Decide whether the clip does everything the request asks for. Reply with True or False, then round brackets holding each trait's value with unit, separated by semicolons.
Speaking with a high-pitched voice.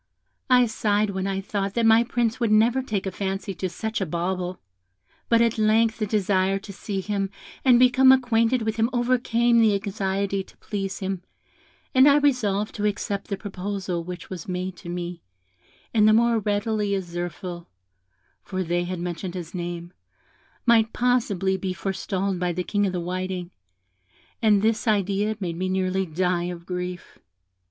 True (195 Hz)